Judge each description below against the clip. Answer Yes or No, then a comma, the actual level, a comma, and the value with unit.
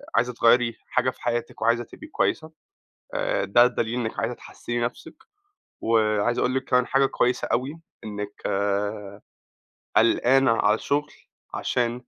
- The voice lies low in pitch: Yes, low, 120 Hz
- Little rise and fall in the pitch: Yes, narrow, 1.9 semitones